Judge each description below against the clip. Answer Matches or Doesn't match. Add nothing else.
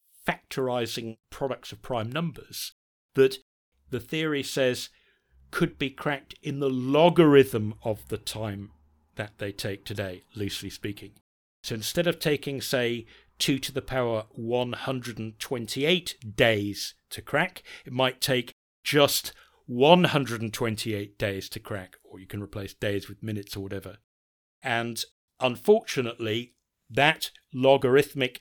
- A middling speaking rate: Doesn't match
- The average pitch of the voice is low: Matches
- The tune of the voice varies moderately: Matches